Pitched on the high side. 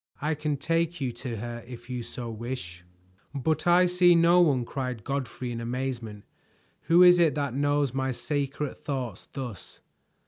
No: low, 135 Hz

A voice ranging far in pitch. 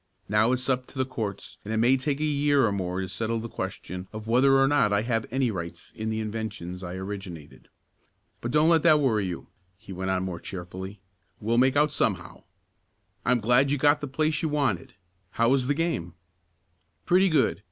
Yes: wide, 6.0 semitones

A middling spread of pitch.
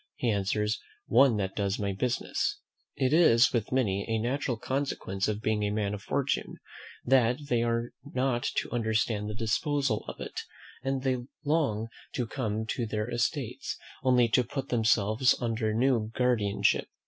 Yes: average, 3.2 semitones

